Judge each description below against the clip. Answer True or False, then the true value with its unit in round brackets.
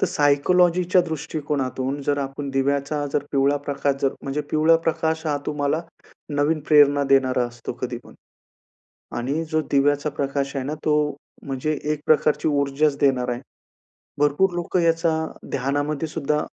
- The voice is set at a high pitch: False (145 Hz)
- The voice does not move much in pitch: True (2.1 semitones)